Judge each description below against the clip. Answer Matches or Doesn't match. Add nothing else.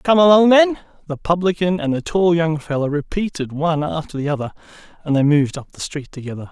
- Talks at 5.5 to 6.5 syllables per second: Matches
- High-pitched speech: Doesn't match